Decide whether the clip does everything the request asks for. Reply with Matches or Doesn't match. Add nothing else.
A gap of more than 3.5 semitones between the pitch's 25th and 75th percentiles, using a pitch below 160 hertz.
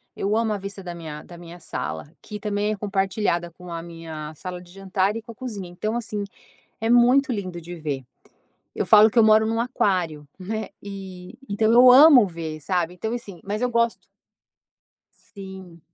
Doesn't match